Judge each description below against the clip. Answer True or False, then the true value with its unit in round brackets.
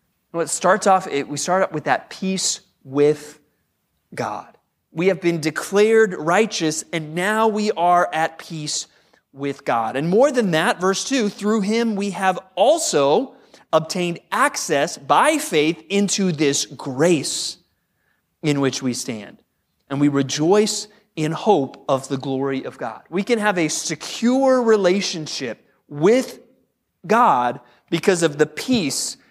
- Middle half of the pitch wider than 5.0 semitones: True (5.5 semitones)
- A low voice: False (175 Hz)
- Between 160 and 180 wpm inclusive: False (140 wpm)